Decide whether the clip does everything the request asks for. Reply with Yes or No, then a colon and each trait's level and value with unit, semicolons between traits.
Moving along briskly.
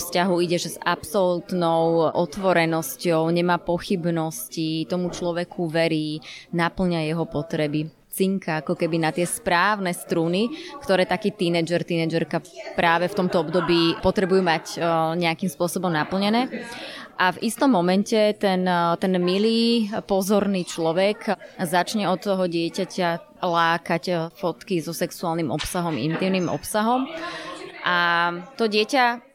No: average, 115 wpm